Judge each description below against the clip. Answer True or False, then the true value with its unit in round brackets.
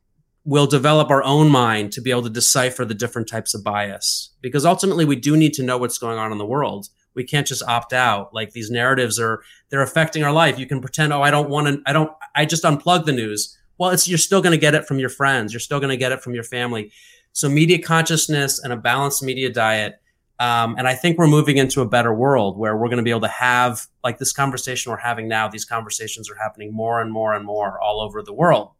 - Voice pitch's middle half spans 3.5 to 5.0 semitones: True (4.3 semitones)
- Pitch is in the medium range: False (125 Hz)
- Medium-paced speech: False (245 wpm)